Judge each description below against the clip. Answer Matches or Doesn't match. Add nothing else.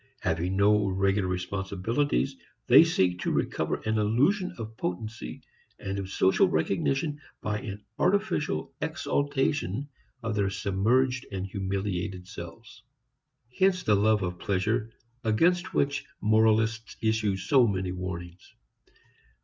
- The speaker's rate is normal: Doesn't match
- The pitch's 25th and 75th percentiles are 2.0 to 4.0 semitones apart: Doesn't match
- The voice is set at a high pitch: Doesn't match